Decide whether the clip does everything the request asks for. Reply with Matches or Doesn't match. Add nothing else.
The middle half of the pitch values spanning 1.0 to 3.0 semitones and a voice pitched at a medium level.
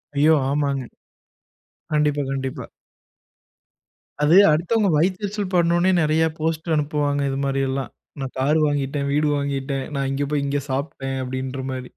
Matches